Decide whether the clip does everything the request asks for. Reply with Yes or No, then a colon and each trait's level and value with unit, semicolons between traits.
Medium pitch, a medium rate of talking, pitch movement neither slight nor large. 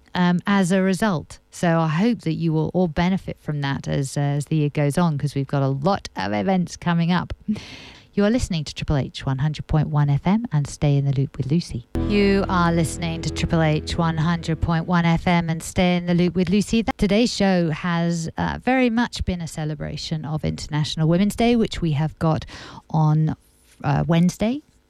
No: medium, 165 Hz; fast, 210 wpm; average, 3.7 semitones